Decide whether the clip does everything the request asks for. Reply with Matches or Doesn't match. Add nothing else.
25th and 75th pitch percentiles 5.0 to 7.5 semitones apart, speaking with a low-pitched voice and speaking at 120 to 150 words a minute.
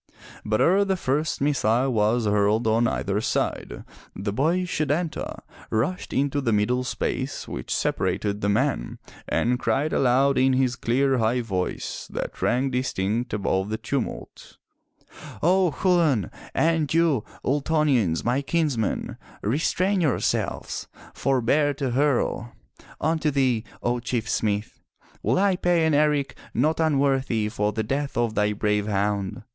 Matches